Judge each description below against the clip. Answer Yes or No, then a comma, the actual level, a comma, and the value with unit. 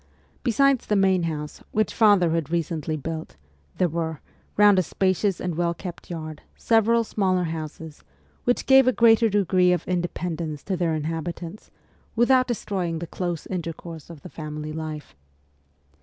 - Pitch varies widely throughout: No, average, 4.0 semitones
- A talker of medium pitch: Yes, medium, 175 Hz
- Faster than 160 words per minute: No, average, 150 wpm